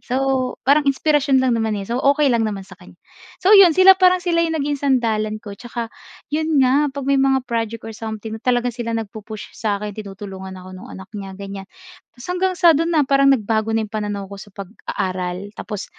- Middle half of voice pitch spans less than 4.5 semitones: No, average, 5.2 semitones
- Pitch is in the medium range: No, high, 230 Hz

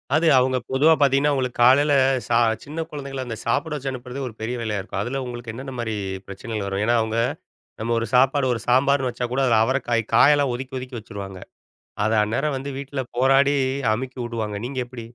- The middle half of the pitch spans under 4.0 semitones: Yes, average, 2.9 semitones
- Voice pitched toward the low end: Yes, low, 125 Hz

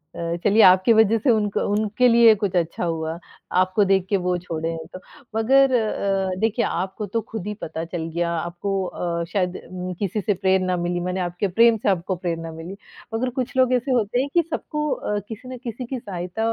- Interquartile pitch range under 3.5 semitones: No, average, 4.3 semitones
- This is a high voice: Yes, high, 195 Hz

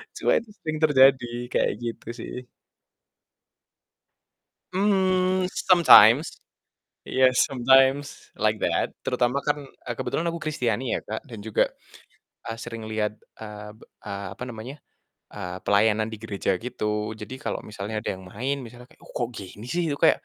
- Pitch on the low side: Yes, low, 120 Hz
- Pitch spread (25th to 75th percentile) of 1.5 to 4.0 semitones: No, average, 4.7 semitones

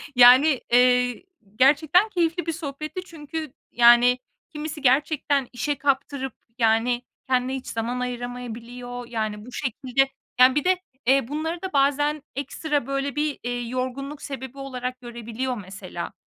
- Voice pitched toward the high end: Yes, very high, 265 Hz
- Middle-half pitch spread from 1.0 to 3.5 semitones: Yes, average, 3.2 semitones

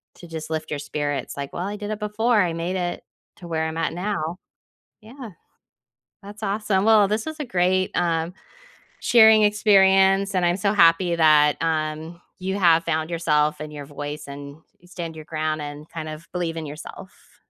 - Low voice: No, medium, 170 Hz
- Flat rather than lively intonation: No, average, 4.2 semitones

